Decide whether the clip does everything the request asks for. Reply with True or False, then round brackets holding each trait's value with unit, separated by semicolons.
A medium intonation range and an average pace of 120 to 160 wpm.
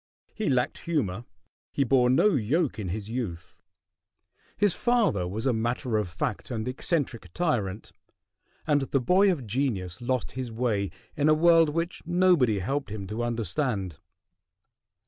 False (6.1 semitones; 145 wpm)